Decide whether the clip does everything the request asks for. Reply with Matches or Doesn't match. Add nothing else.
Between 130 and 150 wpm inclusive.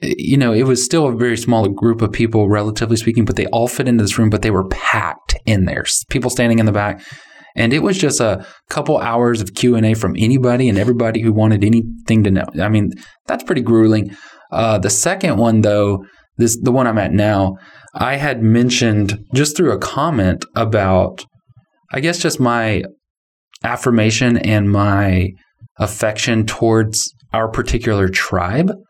Doesn't match